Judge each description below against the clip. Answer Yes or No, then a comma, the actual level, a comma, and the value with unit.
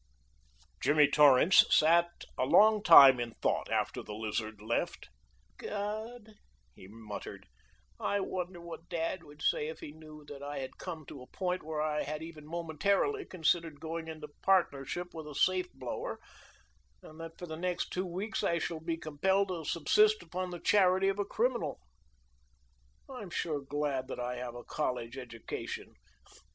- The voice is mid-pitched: Yes, medium, 160 Hz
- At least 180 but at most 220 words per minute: No, average, 165 wpm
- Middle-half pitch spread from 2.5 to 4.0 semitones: No, average, 4.4 semitones